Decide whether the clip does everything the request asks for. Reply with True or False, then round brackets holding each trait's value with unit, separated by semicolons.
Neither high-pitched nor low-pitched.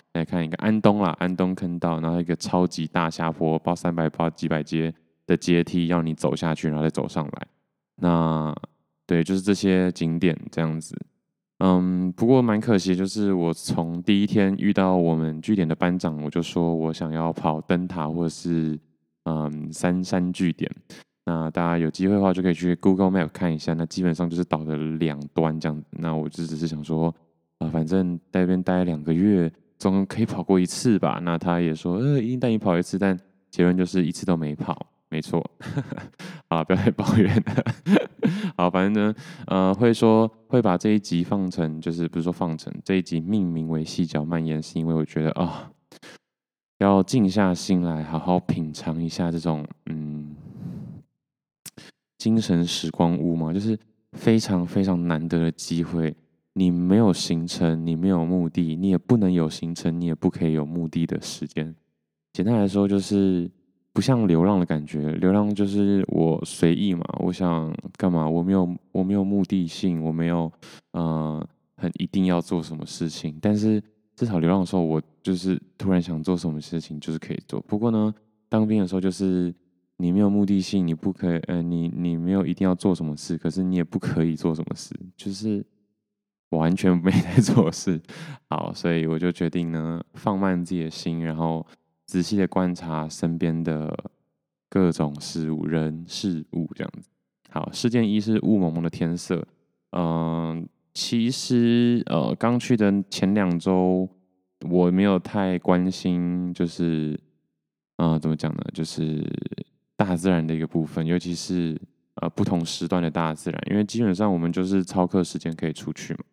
False (85 Hz)